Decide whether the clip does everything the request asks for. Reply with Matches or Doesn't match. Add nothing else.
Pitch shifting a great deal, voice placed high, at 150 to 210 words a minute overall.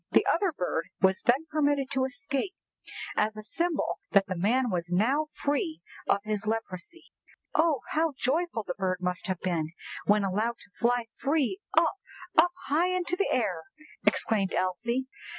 Matches